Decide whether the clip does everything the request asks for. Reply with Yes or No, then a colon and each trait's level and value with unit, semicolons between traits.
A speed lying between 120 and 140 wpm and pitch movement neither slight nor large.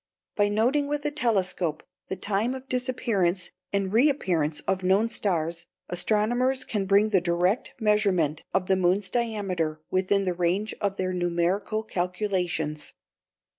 Yes: slow, 135 wpm; average, 3.7 semitones